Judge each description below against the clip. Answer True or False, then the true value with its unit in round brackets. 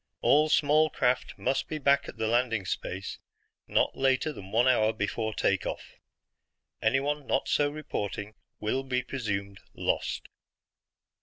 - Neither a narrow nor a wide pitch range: True (4.6 semitones)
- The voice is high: False (125 Hz)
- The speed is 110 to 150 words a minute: True (140 wpm)